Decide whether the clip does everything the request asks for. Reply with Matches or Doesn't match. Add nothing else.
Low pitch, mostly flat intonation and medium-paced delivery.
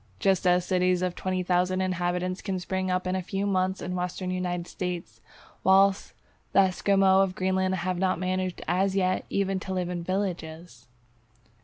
Doesn't match